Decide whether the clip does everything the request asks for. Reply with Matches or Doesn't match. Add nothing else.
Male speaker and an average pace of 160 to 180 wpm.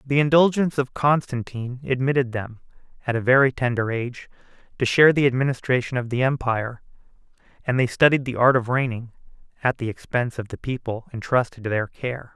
Matches